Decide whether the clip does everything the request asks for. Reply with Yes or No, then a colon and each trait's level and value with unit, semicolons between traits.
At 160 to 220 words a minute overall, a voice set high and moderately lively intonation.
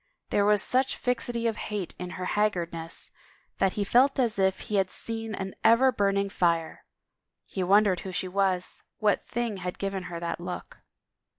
Yes: average, 180 wpm; high, 195 Hz; average, 3.3 semitones